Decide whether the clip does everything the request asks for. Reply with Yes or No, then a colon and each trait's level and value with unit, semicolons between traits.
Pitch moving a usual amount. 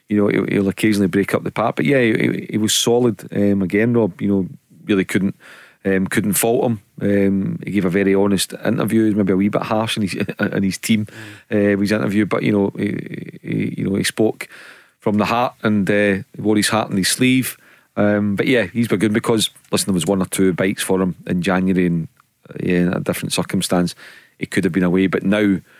No: narrow, 2.1 semitones